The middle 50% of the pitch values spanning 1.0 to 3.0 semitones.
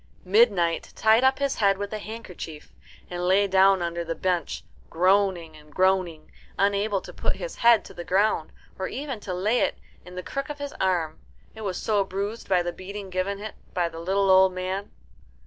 Yes: average, 2.7 semitones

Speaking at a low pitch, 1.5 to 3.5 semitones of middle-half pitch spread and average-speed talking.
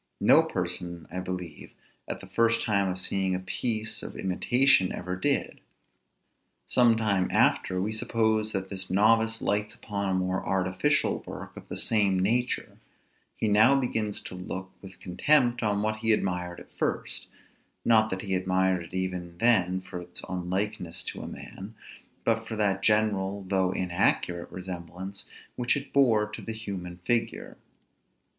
Yes: low, 100 Hz; average, 3.0 semitones; average, 155 wpm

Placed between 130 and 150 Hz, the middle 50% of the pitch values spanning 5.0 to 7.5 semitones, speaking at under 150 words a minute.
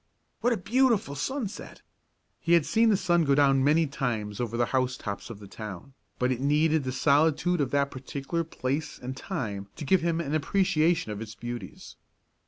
No: medium, 140 Hz; average, 5.3 semitones; average, 185 wpm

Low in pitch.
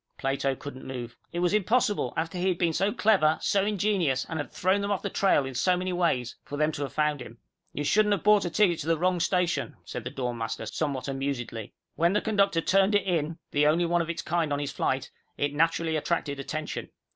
No: medium, 165 Hz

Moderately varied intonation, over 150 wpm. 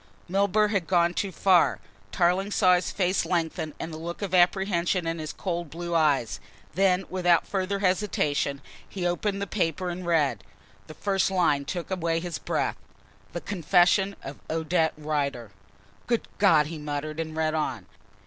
Yes: average, 3.2 semitones; average, 160 wpm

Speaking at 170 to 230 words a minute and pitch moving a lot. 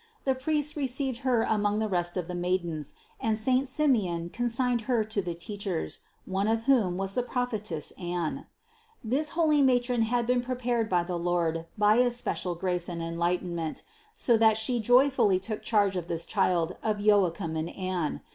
Yes: average, 175 wpm; wide, 5.7 semitones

